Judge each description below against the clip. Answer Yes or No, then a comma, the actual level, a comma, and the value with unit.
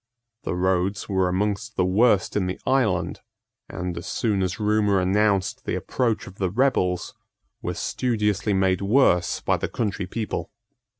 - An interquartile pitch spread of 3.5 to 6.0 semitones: No, narrow, 2.6 semitones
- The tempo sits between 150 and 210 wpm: Yes, average, 155 wpm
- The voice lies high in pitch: No, low, 100 Hz